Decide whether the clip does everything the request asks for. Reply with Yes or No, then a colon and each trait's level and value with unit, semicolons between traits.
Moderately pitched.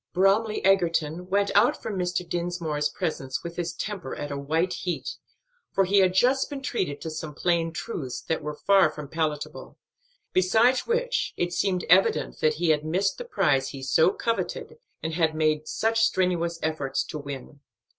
Yes: medium, 175 Hz